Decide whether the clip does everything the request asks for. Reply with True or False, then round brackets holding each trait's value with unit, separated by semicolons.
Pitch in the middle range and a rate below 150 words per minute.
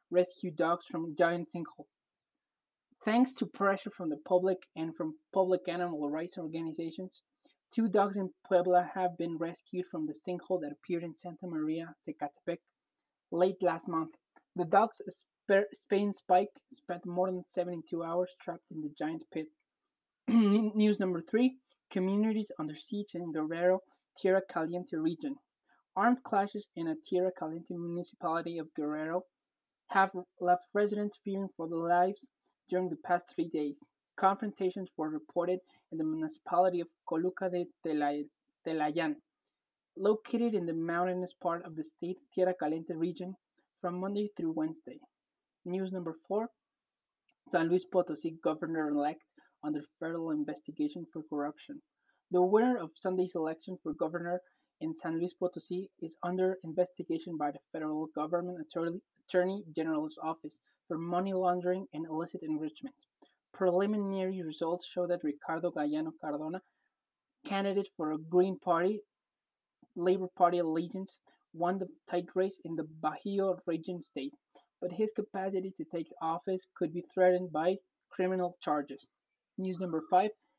True (180 Hz; 140 wpm)